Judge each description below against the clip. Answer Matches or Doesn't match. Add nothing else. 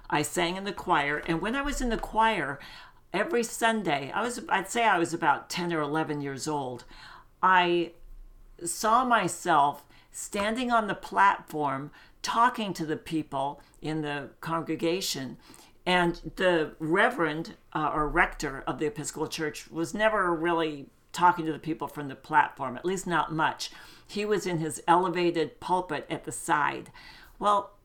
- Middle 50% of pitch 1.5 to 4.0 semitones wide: Matches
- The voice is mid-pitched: Matches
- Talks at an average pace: Matches